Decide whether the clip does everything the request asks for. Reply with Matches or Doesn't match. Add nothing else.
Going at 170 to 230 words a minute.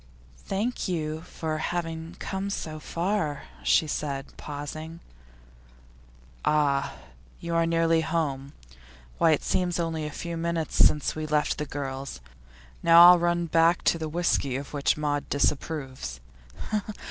Doesn't match